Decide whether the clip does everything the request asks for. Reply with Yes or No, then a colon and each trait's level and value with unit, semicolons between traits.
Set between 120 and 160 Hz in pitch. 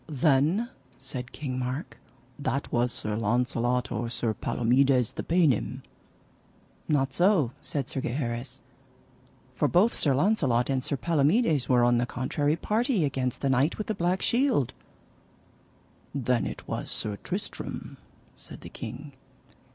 Yes: low, 135 Hz